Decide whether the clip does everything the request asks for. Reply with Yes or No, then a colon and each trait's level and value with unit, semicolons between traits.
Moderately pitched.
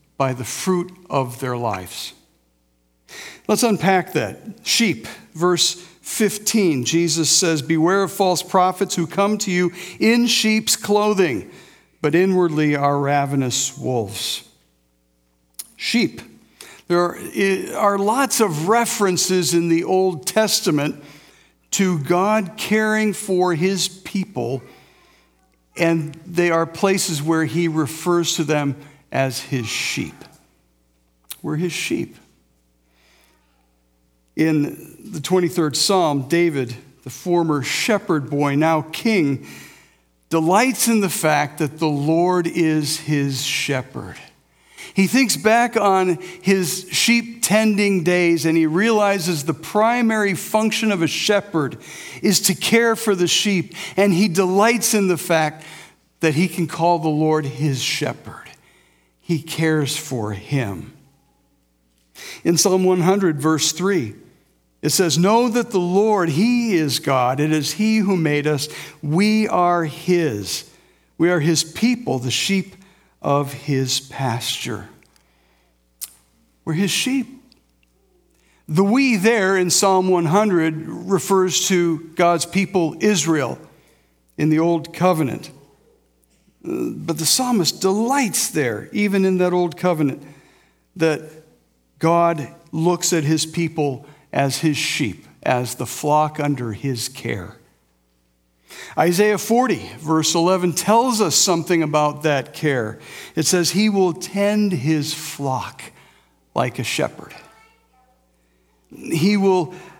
Yes: medium, 165 Hz